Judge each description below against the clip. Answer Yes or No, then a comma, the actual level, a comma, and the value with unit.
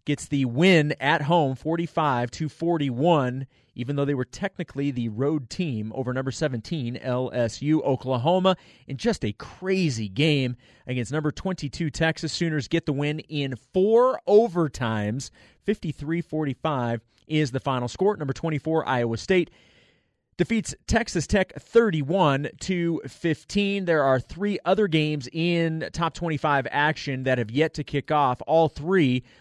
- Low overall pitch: No, medium, 150 Hz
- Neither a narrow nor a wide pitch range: Yes, average, 4.2 semitones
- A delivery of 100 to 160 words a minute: Yes, average, 140 wpm